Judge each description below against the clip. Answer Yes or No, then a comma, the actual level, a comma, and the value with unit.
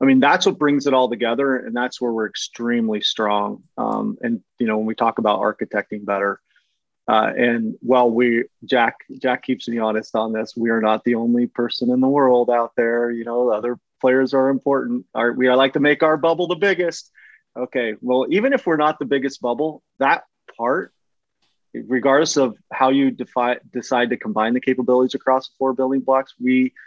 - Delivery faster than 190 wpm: Yes, average, 200 wpm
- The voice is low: Yes, low, 125 Hz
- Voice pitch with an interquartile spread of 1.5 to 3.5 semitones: Yes, narrow, 2.5 semitones